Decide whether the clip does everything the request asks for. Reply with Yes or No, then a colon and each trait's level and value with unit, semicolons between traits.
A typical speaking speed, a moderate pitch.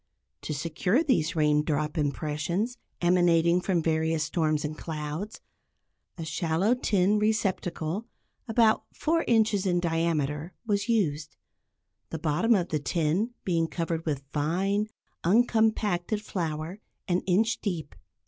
No: slow, 120 wpm; medium, 170 Hz